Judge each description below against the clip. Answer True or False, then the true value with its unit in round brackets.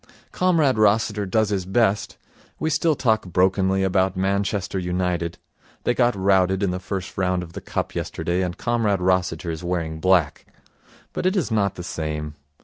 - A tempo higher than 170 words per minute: False (165 wpm)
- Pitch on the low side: True (95 Hz)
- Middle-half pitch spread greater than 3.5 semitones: False (3.1 semitones)